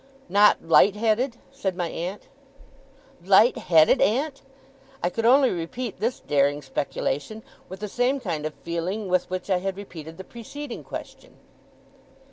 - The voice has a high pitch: Yes, high, 195 Hz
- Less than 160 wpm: Yes, average, 145 wpm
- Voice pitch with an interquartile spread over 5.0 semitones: Yes, wide, 5.4 semitones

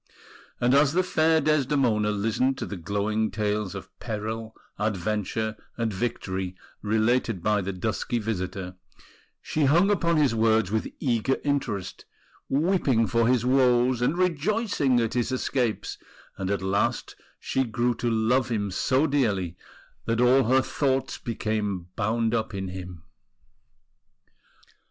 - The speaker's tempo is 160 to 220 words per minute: No, slow, 135 wpm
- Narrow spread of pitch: No, average, 4.1 semitones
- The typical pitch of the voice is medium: No, low, 115 Hz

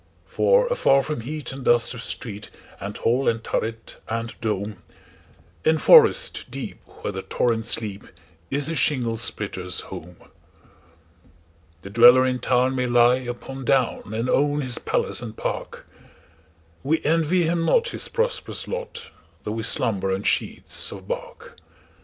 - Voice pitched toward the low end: Yes, low, 120 Hz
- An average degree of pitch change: No, wide, 5.7 semitones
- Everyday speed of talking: No, slow, 130 wpm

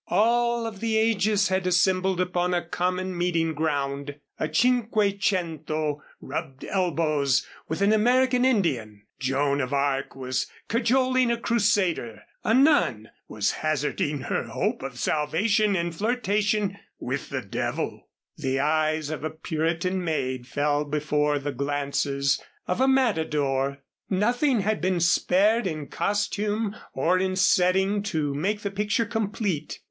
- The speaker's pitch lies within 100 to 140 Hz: No, medium, 180 Hz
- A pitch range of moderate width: No, wide, 6.2 semitones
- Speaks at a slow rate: Yes, slow, 130 wpm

